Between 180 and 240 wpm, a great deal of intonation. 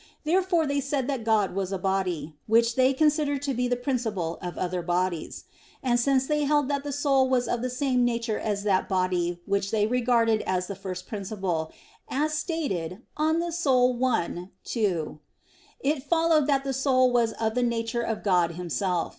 Yes: average, 185 wpm; wide, 6.4 semitones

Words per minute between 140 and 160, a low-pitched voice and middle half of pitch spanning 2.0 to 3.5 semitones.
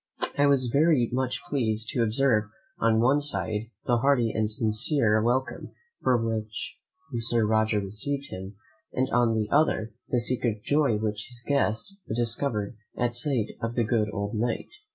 Yes: average, 155 wpm; low, 115 Hz; average, 3.1 semitones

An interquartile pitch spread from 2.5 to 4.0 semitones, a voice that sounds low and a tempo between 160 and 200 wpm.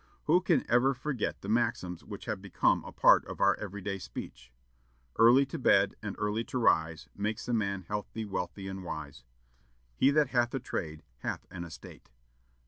No: average, 4.9 semitones; low, 105 Hz; average, 180 wpm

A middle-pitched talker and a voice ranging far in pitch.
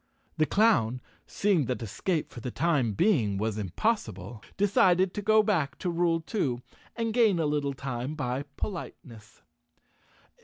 Yes: medium, 150 Hz; wide, 8.1 semitones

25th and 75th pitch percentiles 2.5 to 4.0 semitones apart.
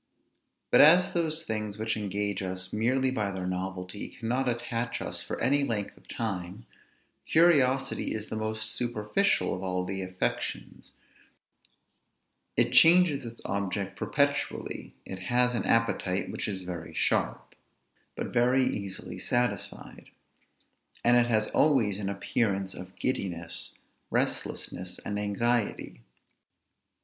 No: average, 4.5 semitones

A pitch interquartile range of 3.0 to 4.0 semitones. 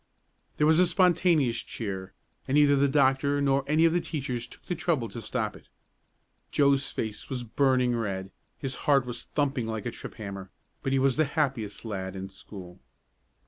No: average, 4.7 semitones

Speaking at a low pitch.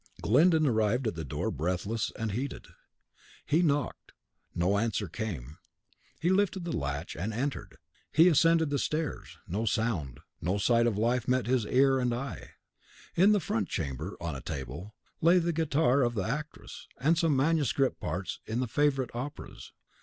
Yes: low, 125 Hz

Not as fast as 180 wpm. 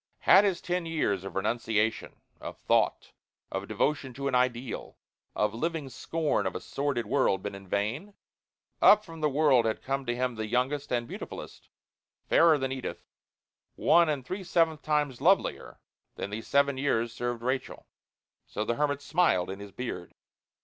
Yes: average, 165 wpm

